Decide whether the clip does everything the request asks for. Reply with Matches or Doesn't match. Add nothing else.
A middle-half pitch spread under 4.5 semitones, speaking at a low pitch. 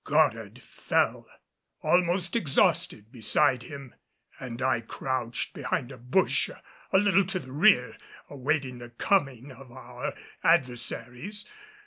Doesn't match